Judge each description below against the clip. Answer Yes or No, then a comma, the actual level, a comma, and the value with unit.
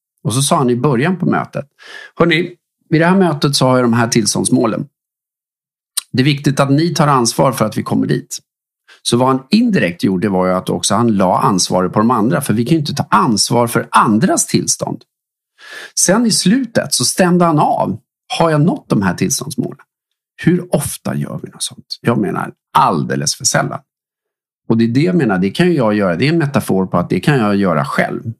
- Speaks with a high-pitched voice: No, medium, 140 Hz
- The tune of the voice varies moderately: No, wide, 7.1 semitones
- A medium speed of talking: No, fast, 210 wpm